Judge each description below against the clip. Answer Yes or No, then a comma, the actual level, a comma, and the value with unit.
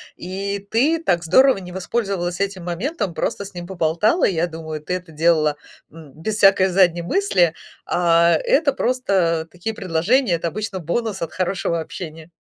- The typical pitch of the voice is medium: Yes, medium, 180 Hz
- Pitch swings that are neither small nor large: Yes, average, 3.3 semitones